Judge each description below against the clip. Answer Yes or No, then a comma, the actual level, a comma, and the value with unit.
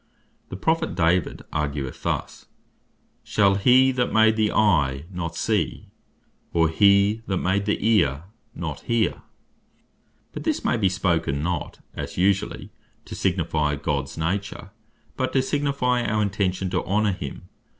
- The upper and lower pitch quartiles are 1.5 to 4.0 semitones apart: No, average, 4.8 semitones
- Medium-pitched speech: No, very low, 95 Hz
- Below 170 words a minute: Yes, average, 140 wpm